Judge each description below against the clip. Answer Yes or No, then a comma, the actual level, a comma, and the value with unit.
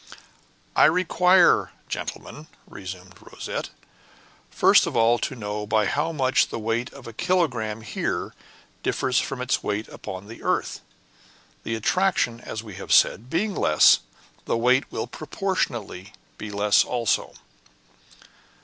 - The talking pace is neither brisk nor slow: No, slow, 130 wpm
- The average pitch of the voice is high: No, low, 115 Hz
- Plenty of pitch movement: Yes, wide, 6.0 semitones